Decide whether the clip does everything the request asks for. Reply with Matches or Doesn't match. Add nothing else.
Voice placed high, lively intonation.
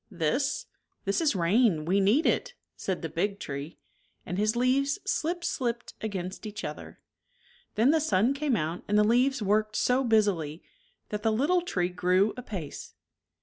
Matches